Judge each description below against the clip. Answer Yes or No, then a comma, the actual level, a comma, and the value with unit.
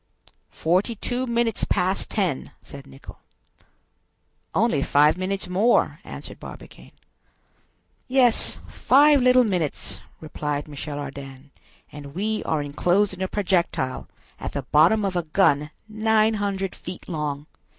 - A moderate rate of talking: No, slow, 120 wpm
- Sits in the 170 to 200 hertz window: Yes, medium, 185 Hz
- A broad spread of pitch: Yes, wide, 6.5 semitones